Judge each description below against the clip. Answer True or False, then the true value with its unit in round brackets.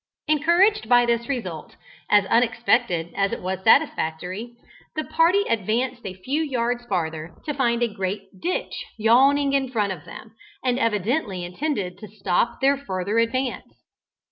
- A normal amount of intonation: False (5.9 semitones)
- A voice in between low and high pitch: False (235 Hz)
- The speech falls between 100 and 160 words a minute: True (145 wpm)